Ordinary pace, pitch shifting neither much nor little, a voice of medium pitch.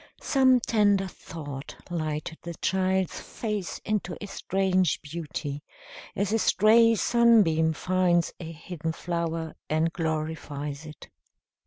No: slow, 115 wpm; average, 4.0 semitones; medium, 175 Hz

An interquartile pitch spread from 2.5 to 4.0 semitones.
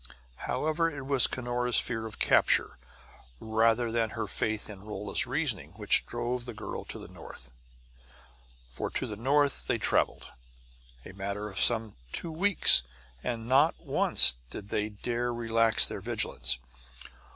Yes: average, 3.2 semitones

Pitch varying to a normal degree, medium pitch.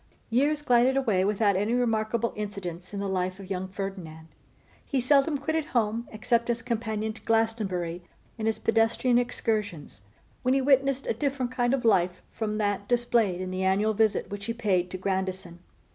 No: average, 4.1 semitones; high, 215 Hz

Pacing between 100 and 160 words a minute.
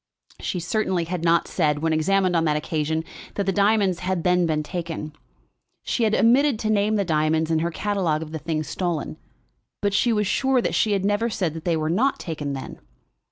No: fast, 205 wpm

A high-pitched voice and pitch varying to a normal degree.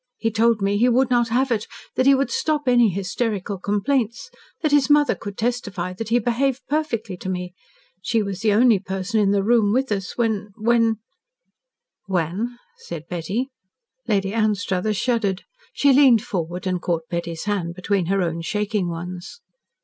Yes: high, 210 Hz; average, 4.3 semitones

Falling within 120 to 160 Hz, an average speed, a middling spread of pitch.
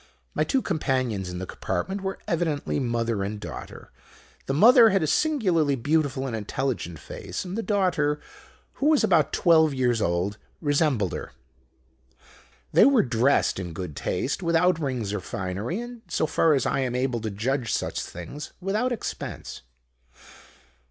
No: medium, 140 Hz; average, 155 wpm; wide, 8.0 semitones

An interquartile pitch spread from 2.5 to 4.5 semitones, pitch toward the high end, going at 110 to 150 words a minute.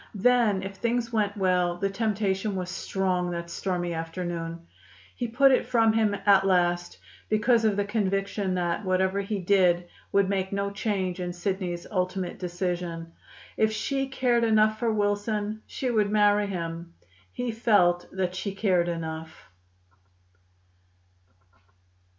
Yes: average, 3.2 semitones; high, 195 Hz; average, 140 wpm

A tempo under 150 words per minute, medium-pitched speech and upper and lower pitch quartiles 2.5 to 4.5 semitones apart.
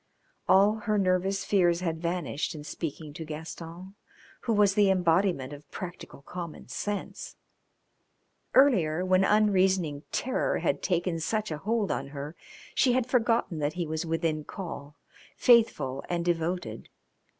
Yes: average, 140 wpm; medium, 175 Hz; average, 4.1 semitones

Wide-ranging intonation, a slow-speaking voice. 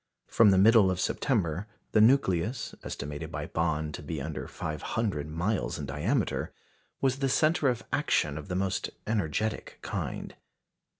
No: wide, 6.4 semitones; average, 155 wpm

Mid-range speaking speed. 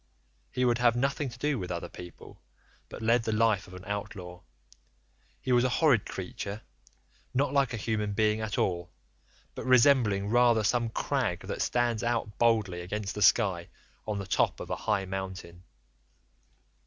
Yes: average, 165 wpm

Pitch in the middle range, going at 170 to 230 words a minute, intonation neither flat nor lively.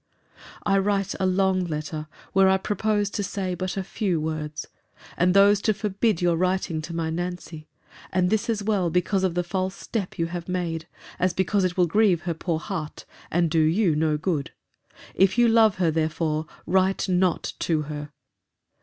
Yes: medium, 180 Hz; average, 180 wpm; average, 3.1 semitones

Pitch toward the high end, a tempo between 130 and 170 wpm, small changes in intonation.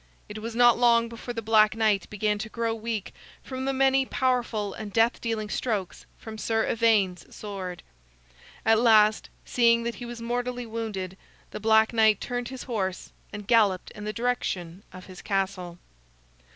Yes: high, 220 Hz; average, 165 wpm; narrow, 2.3 semitones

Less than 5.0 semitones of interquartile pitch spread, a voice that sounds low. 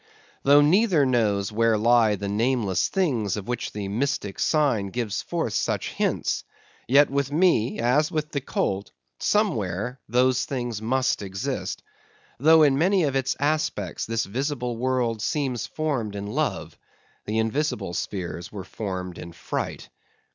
No: wide, 5.5 semitones; low, 120 Hz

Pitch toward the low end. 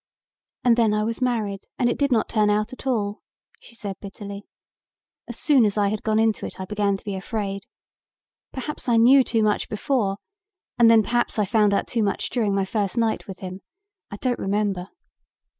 No: high, 215 Hz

